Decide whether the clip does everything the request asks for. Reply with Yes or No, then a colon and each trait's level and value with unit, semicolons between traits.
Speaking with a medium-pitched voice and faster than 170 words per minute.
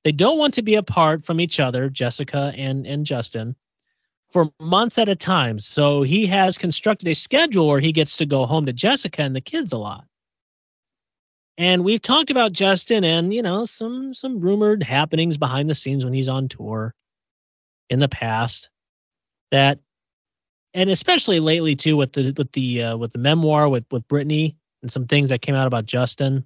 Yes: medium, 150 Hz; average, 190 wpm